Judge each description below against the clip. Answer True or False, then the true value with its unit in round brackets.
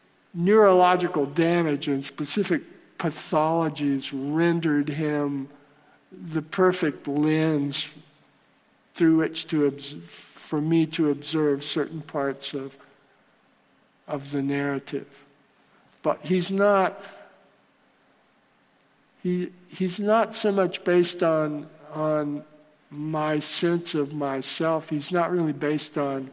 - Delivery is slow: True (100 wpm)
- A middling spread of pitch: True (3.1 semitones)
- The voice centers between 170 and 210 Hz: False (155 Hz)